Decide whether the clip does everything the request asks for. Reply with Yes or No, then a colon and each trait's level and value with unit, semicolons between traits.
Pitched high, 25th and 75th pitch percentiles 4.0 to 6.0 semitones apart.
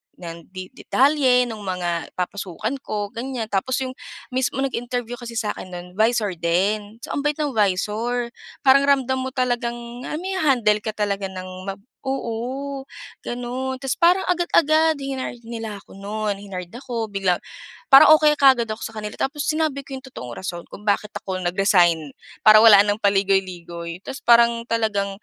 Yes: high, 230 Hz; average, 5.0 semitones